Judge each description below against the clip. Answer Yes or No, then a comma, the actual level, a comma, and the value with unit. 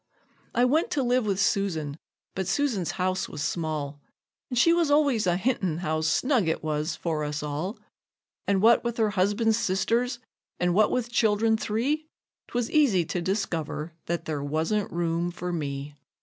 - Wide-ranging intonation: Yes, wide, 6.5 semitones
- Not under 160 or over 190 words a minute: Yes, average, 165 wpm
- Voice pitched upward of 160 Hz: Yes, high, 190 Hz